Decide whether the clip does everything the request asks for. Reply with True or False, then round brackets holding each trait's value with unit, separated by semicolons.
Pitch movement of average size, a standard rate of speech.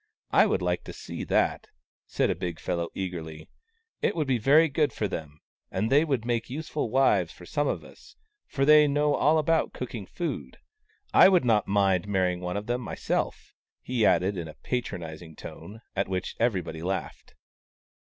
False (7.7 semitones; 190 wpm)